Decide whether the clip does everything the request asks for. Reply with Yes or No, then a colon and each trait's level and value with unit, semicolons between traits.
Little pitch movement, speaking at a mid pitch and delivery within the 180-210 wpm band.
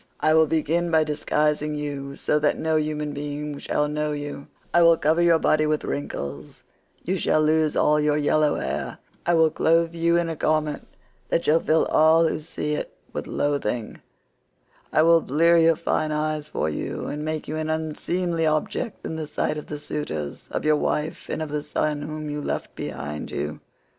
Yes: narrow, 1.4 semitones; medium, 155 Hz; average, 190 wpm